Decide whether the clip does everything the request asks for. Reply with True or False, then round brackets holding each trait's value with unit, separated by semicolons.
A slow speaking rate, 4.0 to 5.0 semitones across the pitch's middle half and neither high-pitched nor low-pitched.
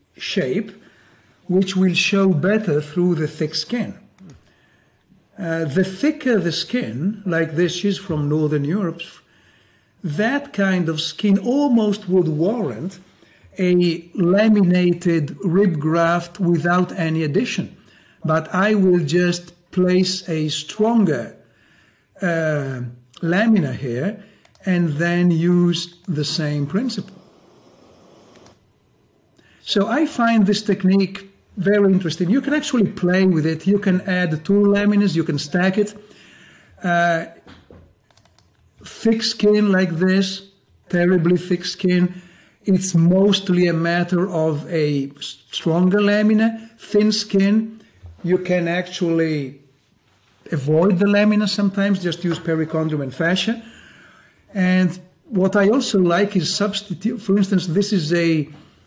False (115 wpm; 3.5 semitones; 180 Hz)